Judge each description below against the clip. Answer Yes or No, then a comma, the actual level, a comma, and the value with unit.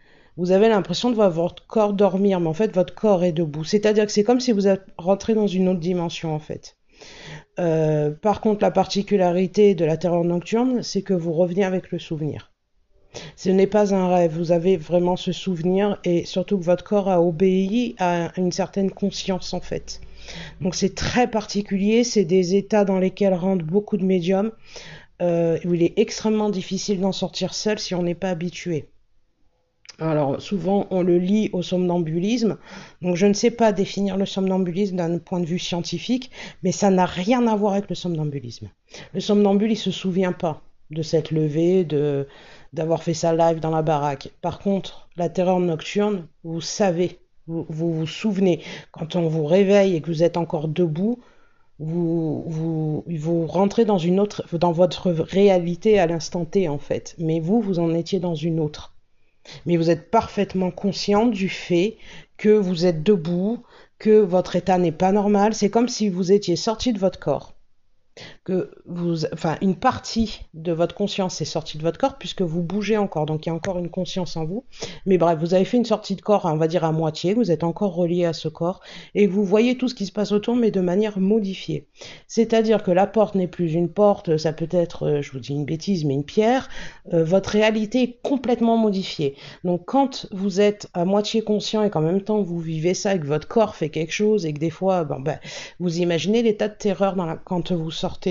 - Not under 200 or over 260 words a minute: Yes, average, 205 wpm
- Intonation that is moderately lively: Yes, average, 3.4 semitones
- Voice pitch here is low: No, medium, 185 Hz